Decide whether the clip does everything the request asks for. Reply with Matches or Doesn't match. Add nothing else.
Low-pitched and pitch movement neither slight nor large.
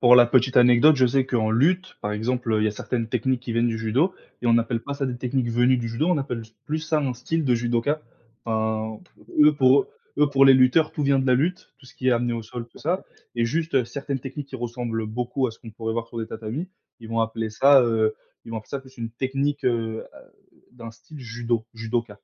Matches